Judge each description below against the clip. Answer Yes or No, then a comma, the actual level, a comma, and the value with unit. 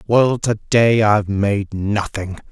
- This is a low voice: Yes, low, 105 Hz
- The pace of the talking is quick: No, average, 145 wpm